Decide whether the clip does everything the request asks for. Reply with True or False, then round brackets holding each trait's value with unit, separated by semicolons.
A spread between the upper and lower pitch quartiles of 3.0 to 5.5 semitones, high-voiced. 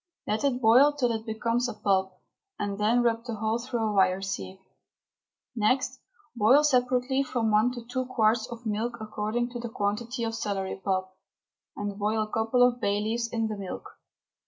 False (2.6 semitones; 225 Hz)